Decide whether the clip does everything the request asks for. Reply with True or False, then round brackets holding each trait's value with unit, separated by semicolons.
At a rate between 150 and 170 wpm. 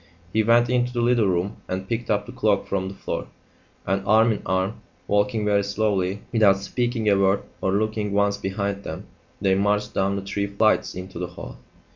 False (195 wpm)